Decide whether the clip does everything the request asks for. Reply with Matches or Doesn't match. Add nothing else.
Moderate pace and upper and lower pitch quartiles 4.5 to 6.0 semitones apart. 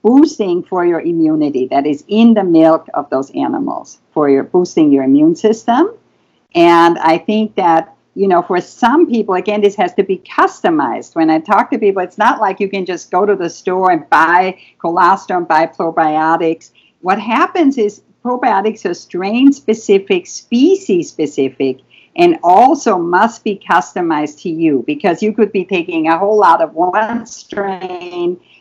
Matches